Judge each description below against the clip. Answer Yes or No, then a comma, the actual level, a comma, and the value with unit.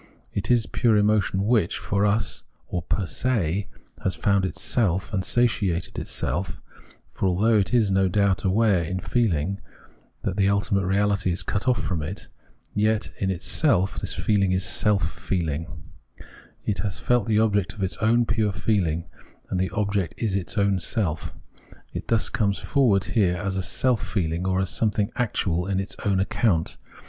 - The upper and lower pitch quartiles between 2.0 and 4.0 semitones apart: Yes, narrow, 2.6 semitones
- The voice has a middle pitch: No, low, 100 Hz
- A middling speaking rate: Yes, average, 165 wpm